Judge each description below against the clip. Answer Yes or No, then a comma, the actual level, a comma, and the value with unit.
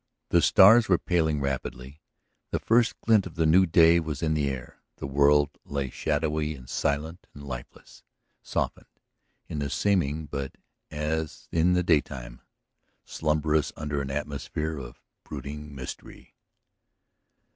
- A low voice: Yes, very low, 75 Hz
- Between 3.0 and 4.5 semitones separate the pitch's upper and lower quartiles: No, narrow, 2.6 semitones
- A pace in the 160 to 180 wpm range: No, slow, 135 wpm